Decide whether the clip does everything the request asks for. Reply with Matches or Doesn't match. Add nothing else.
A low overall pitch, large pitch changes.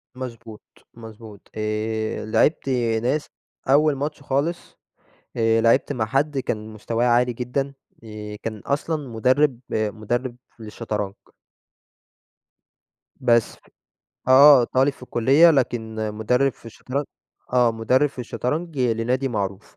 Doesn't match